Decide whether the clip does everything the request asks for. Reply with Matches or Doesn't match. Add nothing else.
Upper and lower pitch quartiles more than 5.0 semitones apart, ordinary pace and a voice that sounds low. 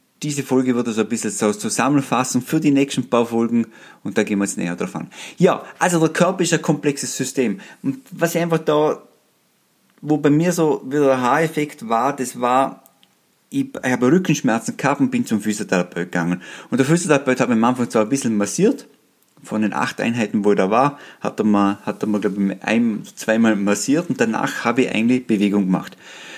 Doesn't match